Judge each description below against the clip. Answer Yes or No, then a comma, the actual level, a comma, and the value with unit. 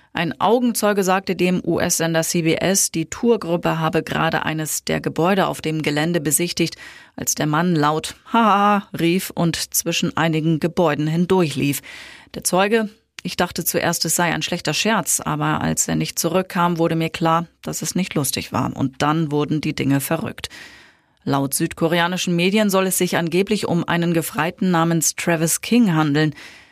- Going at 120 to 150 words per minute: No, average, 160 wpm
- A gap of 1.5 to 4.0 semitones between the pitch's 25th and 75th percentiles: Yes, average, 2.8 semitones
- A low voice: No, medium, 165 Hz